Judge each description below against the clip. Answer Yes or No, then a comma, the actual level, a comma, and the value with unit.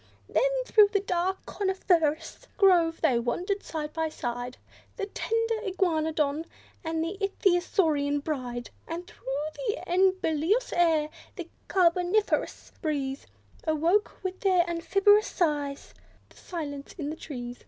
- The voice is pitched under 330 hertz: No, very high, 335 Hz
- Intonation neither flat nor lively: Yes, average, 4.2 semitones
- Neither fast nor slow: No, slow, 120 wpm